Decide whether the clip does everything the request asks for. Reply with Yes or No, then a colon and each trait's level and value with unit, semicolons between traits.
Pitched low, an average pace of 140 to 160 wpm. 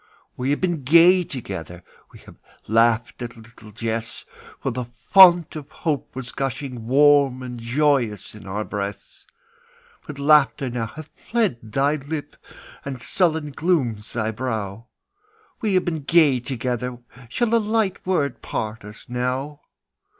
Yes: low, 130 Hz; average, 145 wpm